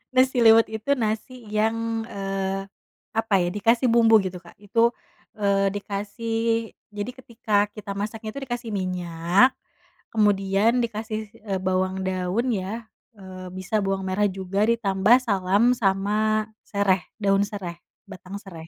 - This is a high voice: Yes, high, 200 Hz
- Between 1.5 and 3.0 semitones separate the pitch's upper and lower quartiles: Yes, average, 2.7 semitones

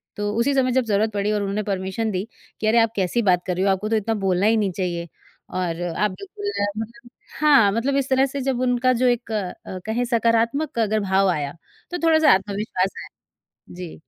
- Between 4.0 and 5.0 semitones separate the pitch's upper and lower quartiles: Yes, average, 4.3 semitones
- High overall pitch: Yes, high, 220 Hz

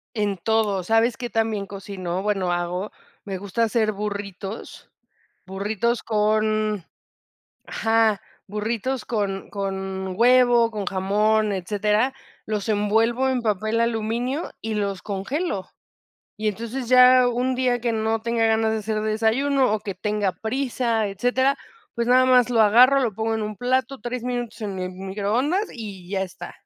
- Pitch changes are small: No, average, 3.0 semitones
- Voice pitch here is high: Yes, high, 220 Hz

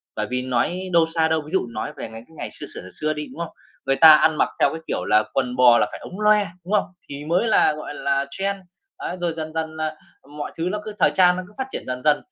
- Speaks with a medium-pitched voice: Yes, medium, 155 Hz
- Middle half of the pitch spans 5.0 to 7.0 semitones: No, average, 4.5 semitones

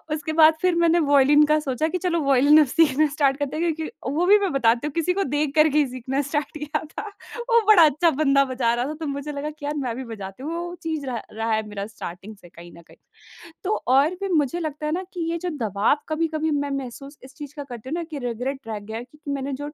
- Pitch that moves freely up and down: No, average, 3.4 semitones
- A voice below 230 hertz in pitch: No, very high, 290 Hz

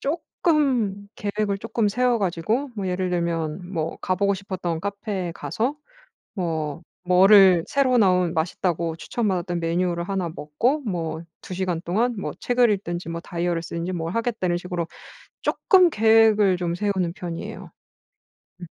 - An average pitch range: Yes, average, 3.9 semitones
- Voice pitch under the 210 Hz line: Yes, medium, 185 Hz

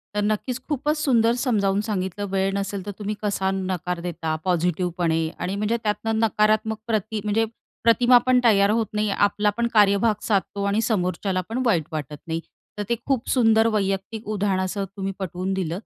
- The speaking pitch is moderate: No, high, 205 Hz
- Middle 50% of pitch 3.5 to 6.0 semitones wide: No, average, 2.9 semitones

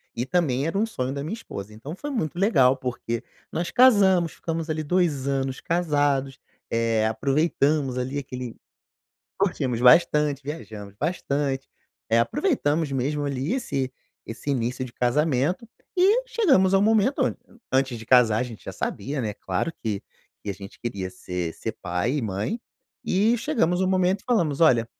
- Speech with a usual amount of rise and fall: No, wide, 6.3 semitones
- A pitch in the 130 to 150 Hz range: Yes, medium, 140 Hz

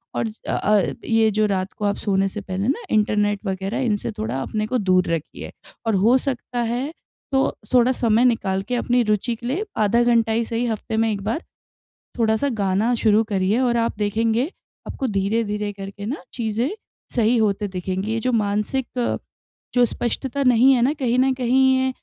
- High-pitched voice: Yes, high, 225 Hz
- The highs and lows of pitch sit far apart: No, average, 3.1 semitones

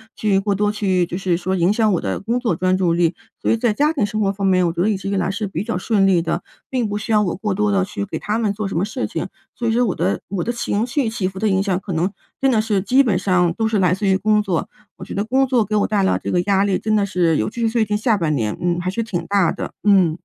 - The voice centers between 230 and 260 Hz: No, high, 200 Hz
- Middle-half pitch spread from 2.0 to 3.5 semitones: Yes, average, 2.9 semitones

